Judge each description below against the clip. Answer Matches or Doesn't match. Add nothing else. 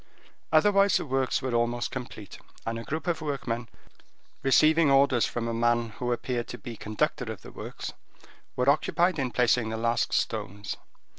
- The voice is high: Doesn't match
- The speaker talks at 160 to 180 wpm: Matches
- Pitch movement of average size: Matches